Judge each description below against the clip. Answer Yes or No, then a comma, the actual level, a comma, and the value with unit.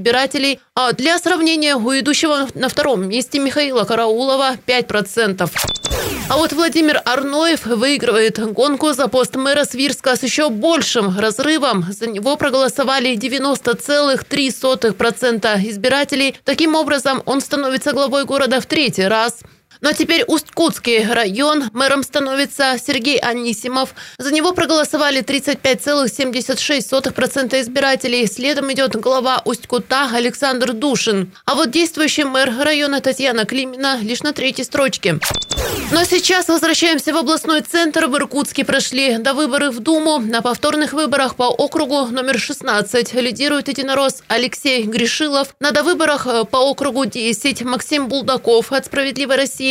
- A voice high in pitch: Yes, very high, 270 Hz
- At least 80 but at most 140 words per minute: Yes, average, 130 wpm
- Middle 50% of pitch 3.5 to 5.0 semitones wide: No, average, 2.9 semitones